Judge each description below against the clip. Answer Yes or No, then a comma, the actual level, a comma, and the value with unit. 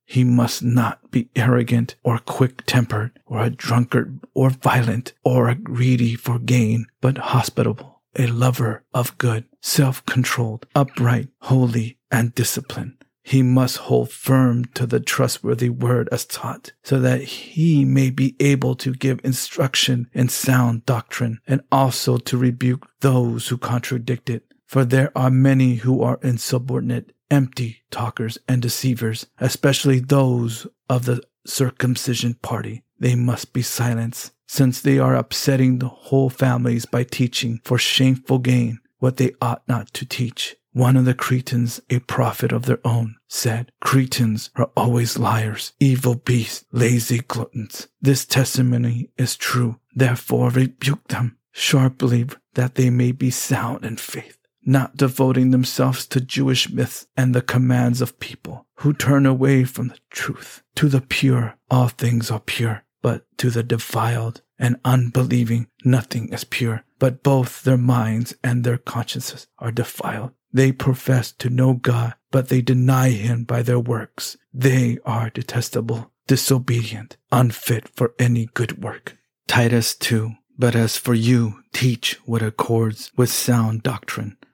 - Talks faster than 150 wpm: No, average, 145 wpm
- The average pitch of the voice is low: Yes, low, 125 Hz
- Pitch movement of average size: No, narrow, 1.6 semitones